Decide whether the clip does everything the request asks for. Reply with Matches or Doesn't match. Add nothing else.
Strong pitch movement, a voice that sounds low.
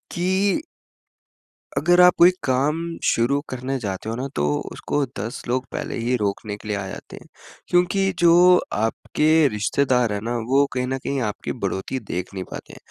Matches